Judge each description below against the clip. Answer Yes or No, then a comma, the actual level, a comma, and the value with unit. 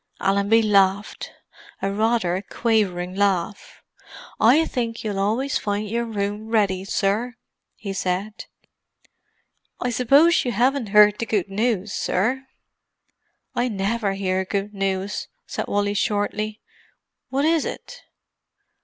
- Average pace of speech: No, slow, 115 wpm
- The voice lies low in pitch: No, high, 210 Hz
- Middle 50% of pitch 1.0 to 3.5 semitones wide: Yes, average, 2.9 semitones